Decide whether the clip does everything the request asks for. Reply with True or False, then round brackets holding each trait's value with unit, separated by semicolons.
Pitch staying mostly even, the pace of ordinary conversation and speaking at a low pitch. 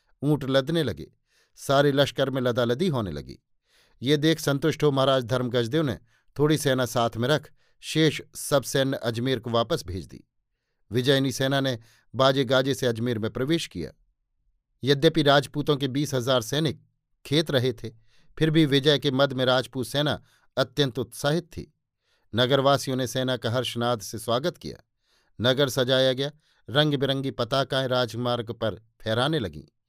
False (3.0 semitones; 155 wpm; 130 Hz)